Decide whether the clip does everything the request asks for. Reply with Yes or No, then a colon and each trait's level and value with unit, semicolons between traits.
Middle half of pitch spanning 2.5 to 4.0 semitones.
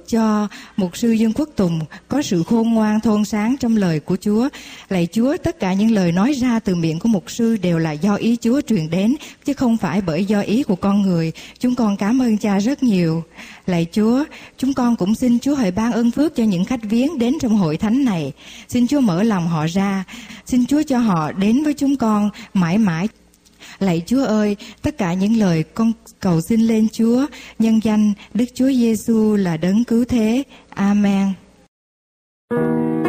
Yes: average, 3.7 semitones